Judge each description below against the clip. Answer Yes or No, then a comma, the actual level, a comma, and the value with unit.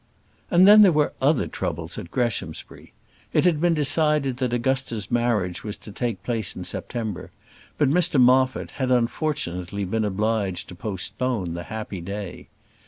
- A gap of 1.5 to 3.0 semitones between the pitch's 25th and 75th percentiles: No, wide, 5.4 semitones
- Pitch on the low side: Yes, low, 120 Hz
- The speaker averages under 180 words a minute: Yes, average, 155 wpm